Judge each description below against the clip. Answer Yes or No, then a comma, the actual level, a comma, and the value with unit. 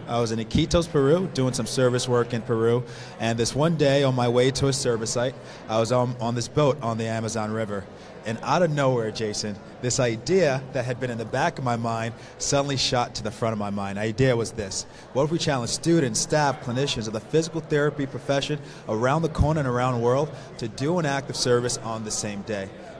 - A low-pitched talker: Yes, low, 125 Hz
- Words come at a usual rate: No, fast, 230 wpm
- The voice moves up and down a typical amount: Yes, average, 3.6 semitones